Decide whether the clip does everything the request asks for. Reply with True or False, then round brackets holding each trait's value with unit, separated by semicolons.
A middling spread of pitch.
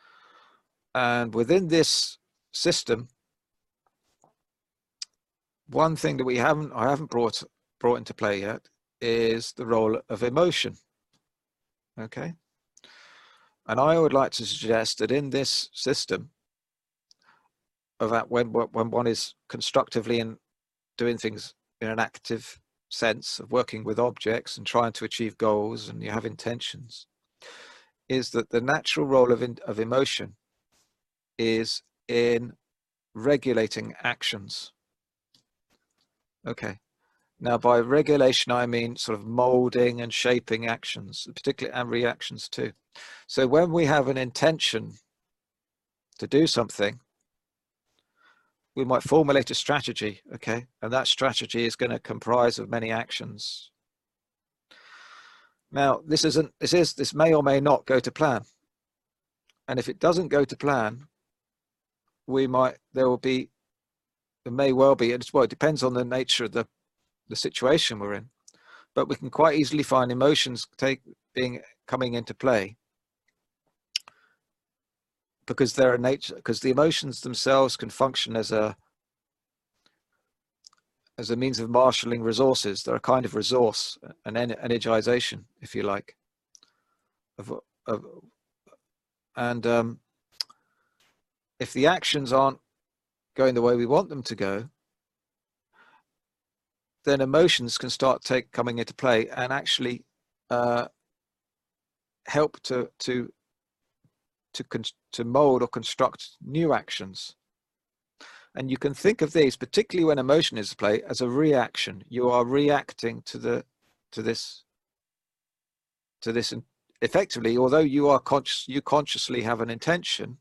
True (3.2 semitones)